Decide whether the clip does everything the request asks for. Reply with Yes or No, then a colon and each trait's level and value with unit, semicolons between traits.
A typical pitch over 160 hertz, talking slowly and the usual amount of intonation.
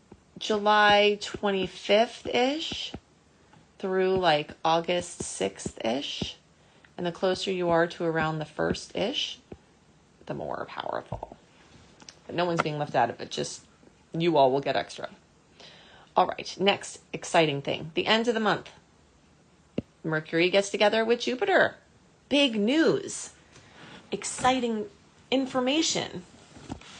Yes: high, 190 Hz; slow, 120 wpm; average, 4.8 semitones